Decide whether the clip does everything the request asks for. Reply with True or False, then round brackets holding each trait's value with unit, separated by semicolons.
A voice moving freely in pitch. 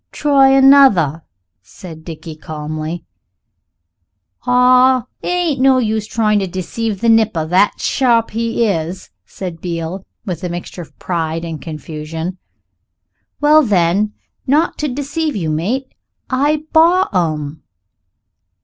True (7.8 semitones)